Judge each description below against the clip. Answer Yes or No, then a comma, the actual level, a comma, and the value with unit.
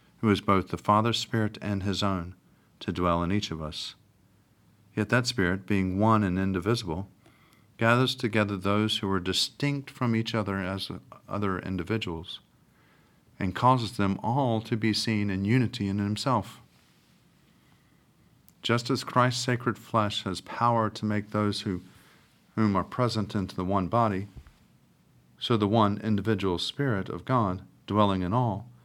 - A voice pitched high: No, low, 105 Hz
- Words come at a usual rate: Yes, average, 150 wpm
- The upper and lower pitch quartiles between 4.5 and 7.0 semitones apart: No, average, 3.3 semitones